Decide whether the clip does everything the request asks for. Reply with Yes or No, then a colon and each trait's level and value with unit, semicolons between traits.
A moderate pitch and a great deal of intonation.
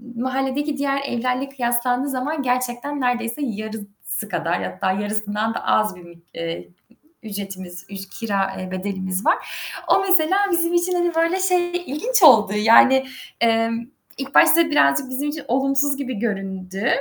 No: high, 245 Hz; wide, 5.8 semitones